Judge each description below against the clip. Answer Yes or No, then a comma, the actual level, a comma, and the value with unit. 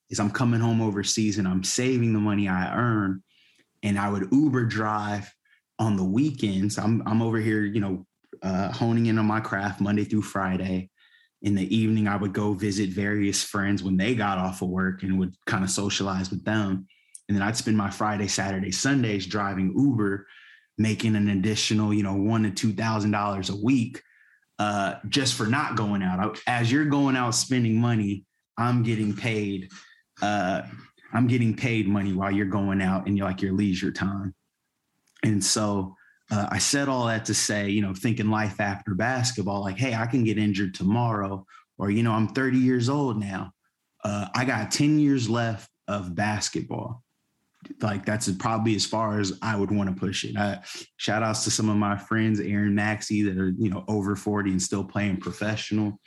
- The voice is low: Yes, low, 105 Hz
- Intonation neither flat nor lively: No, narrow, 2.1 semitones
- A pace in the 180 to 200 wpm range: Yes, average, 190 wpm